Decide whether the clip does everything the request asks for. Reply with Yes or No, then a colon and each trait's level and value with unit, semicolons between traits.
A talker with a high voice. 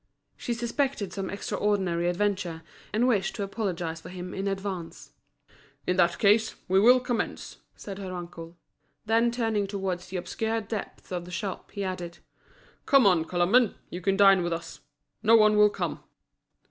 Yes: high, 195 Hz